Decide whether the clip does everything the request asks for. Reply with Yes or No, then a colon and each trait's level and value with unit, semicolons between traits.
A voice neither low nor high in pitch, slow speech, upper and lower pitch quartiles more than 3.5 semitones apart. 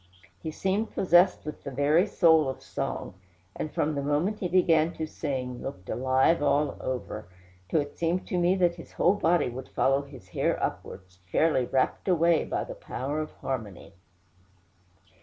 No: medium, 155 Hz; average, 170 wpm; average, 4.7 semitones